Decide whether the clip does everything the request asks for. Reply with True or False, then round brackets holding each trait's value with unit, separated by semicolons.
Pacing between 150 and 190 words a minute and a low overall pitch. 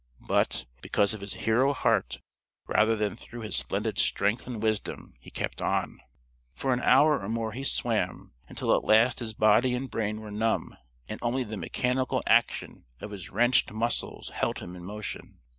True (175 wpm; 110 Hz)